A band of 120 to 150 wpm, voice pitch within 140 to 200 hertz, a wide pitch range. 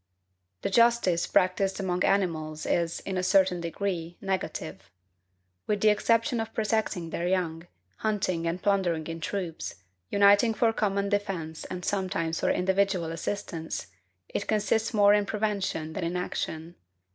No: average, 140 wpm; high, 190 Hz; average, 3.3 semitones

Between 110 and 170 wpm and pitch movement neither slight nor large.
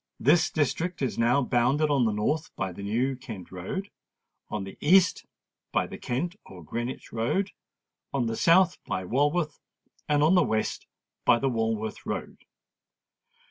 No: average, 155 wpm; wide, 6.0 semitones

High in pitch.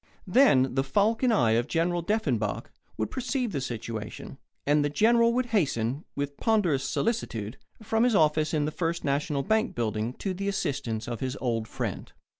No: medium, 150 Hz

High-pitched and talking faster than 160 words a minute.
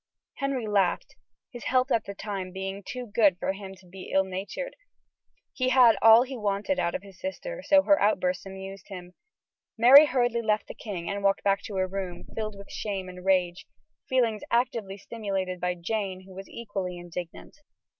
Yes: high, 200 Hz; average, 185 wpm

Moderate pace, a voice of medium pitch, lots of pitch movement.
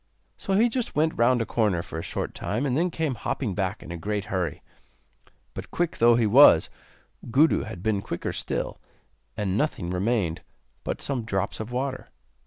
No: average, 185 wpm; low, 115 Hz; wide, 6.2 semitones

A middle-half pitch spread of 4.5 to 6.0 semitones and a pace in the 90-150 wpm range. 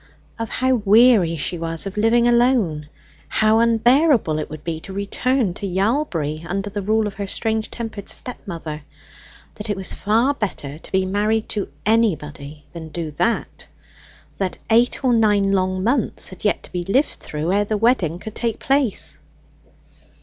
No: average, 4.8 semitones; average, 170 wpm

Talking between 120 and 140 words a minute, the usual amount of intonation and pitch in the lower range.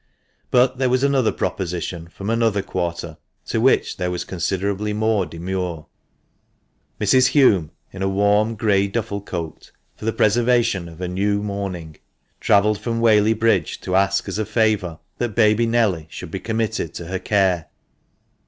No: average, 155 wpm; average, 3.6 semitones; low, 100 Hz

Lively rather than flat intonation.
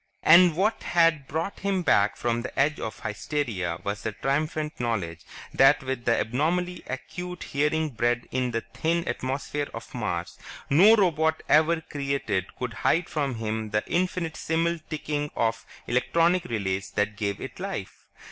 Yes: wide, 6.4 semitones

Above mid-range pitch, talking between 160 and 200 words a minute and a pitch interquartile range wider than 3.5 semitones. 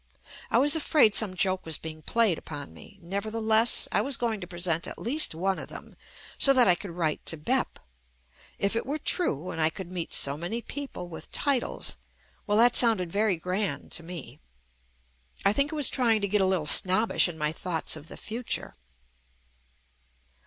Yes: high, 195 Hz; average, 190 wpm; wide, 5.5 semitones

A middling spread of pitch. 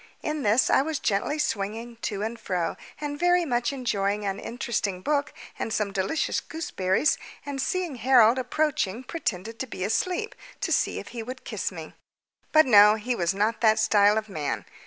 No: wide, 5.7 semitones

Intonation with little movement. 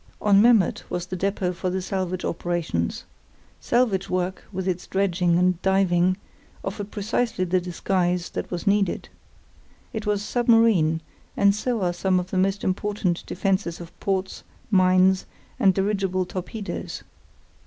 Yes: narrow, 2.0 semitones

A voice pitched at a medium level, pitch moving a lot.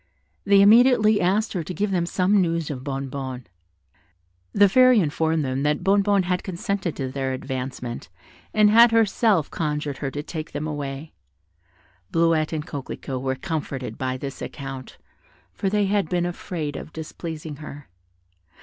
Yes: medium, 160 Hz; wide, 6.1 semitones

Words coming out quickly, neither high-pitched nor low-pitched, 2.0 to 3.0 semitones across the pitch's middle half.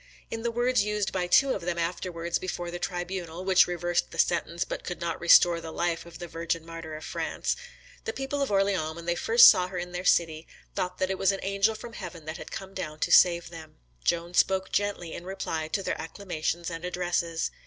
Yes: fast, 220 wpm; medium, 175 Hz; narrow, 2.4 semitones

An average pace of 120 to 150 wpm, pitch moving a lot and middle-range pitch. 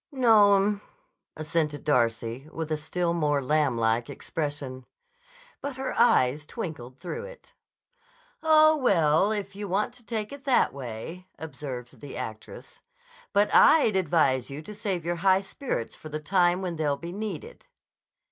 Yes: average, 145 wpm; wide, 6.3 semitones; medium, 170 Hz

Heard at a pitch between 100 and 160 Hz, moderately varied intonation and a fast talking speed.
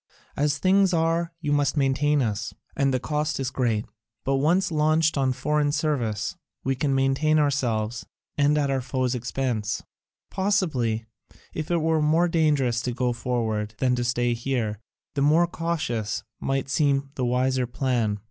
No: low, 135 Hz; average, 3.8 semitones; average, 155 wpm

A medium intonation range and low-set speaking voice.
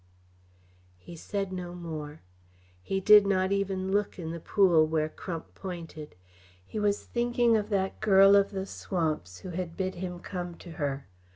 No: average, 3.2 semitones; medium, 185 Hz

